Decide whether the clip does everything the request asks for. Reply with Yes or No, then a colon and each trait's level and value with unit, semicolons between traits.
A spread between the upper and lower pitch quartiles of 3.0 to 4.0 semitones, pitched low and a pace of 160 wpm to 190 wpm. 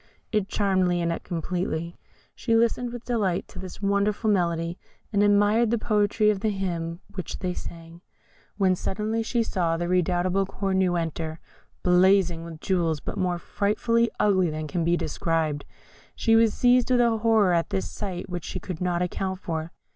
No: average, 3.7 semitones; medium, 185 Hz; average, 170 wpm